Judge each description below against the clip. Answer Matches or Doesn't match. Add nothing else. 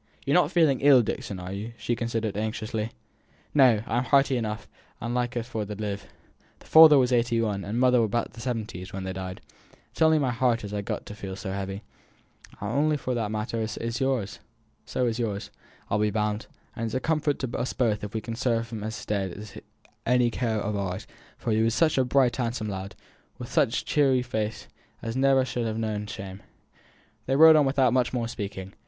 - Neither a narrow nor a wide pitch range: Matches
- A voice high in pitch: Doesn't match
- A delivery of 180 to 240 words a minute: Matches